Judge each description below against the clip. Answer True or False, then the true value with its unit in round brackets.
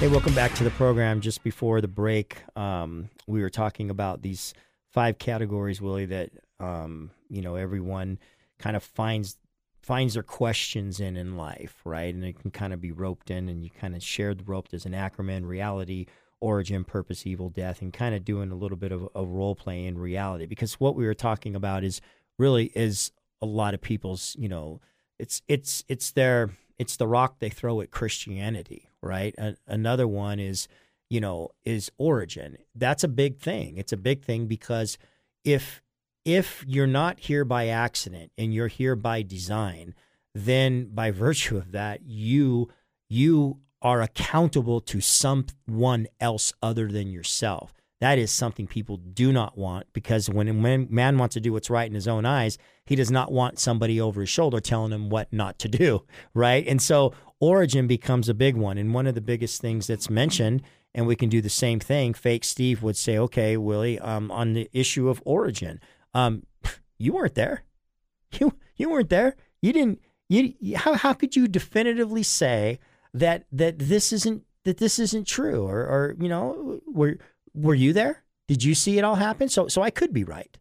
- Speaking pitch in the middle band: False (115 Hz)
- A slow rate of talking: False (190 wpm)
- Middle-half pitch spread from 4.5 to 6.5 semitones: True (4.9 semitones)